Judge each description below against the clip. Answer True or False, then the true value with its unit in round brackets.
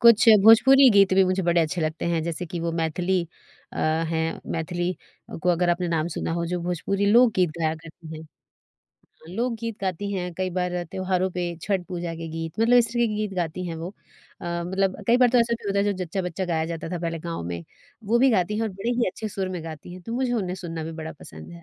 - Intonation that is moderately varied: True (3.4 semitones)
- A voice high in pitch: False (180 Hz)